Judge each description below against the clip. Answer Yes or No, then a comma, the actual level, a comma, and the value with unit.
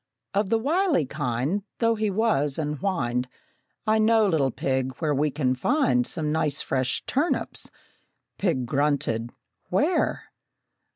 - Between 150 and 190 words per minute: No, slow, 135 wpm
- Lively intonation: Yes, wide, 8.5 semitones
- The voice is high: No, medium, 155 Hz